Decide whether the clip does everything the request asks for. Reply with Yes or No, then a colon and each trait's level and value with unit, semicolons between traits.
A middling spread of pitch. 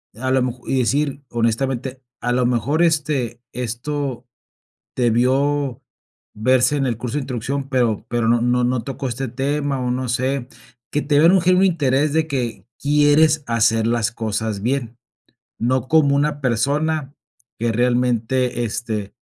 Yes: average, 3.2 semitones